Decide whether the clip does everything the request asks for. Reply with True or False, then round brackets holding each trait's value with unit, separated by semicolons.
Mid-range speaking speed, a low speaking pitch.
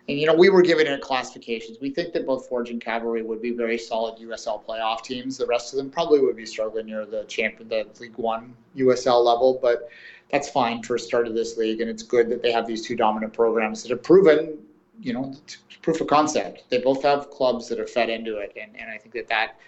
False (245 wpm; 120 Hz)